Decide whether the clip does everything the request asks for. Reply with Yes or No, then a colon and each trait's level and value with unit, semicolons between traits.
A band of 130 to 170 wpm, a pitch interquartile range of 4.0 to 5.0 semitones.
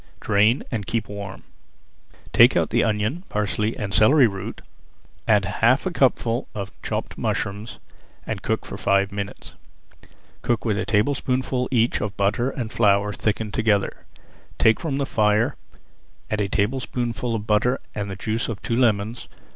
No: average, 155 wpm; average, 2.8 semitones